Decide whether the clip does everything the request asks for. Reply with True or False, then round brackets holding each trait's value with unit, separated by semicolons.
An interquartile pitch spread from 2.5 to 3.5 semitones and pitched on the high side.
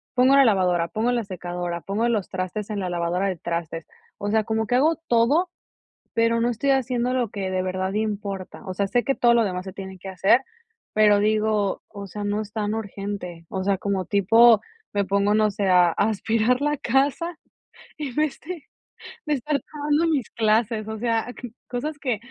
False (4.0 semitones; 215 Hz)